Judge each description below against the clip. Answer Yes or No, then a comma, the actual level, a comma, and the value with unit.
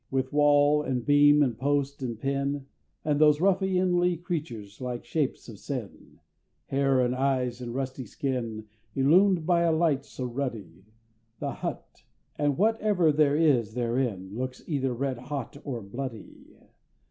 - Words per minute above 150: No, average, 145 wpm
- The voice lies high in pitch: No, low, 135 Hz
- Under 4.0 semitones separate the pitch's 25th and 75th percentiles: Yes, average, 3.4 semitones